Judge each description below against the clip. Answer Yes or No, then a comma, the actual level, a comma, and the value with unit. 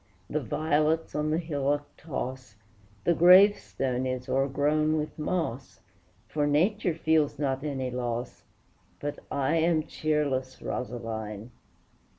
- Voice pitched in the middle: Yes, medium, 145 Hz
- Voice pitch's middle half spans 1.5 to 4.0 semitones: Yes, average, 3.4 semitones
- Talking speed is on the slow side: Yes, slow, 115 wpm